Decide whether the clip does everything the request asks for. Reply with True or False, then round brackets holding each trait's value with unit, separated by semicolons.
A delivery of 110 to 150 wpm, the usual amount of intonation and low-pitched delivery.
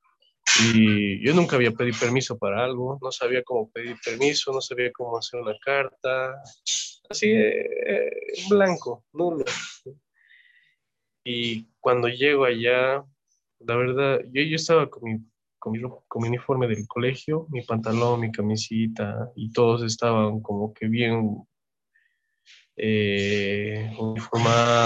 True (130 wpm; 3.7 semitones; 120 Hz)